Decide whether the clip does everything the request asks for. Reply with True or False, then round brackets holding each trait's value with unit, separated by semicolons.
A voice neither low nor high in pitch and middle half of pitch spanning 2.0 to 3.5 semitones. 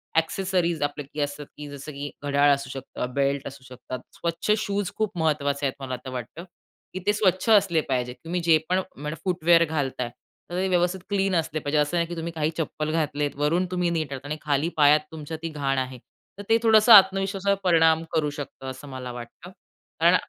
False (155 Hz; 4.0 semitones)